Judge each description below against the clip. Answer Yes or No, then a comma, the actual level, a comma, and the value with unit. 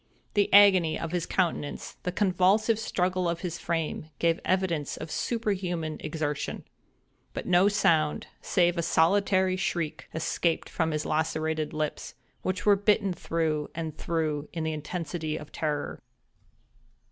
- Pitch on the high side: No, medium, 170 Hz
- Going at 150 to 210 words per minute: No, slow, 135 wpm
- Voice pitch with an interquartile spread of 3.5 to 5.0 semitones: No, average, 3.0 semitones